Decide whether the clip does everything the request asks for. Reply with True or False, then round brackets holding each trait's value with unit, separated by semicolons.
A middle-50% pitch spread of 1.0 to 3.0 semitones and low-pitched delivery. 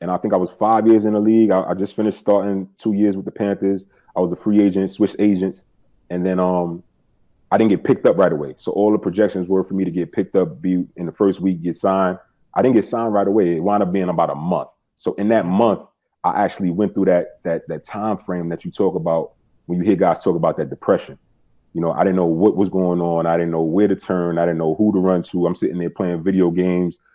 True (2.5 semitones; 95 Hz)